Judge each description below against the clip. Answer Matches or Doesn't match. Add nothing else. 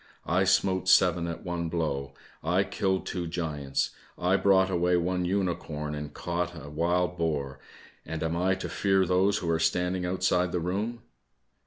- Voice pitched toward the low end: Matches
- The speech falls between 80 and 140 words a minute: Doesn't match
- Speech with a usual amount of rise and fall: Doesn't match